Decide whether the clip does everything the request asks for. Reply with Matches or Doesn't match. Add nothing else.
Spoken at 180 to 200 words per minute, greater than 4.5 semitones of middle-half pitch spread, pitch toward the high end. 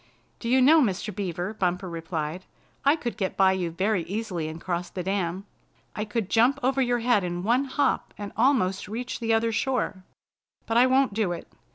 Matches